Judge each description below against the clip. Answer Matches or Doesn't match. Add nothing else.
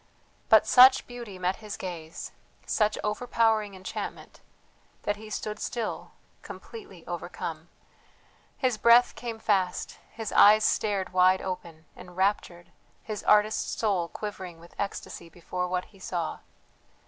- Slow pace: Matches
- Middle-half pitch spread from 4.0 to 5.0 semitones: Doesn't match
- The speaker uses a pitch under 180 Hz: Doesn't match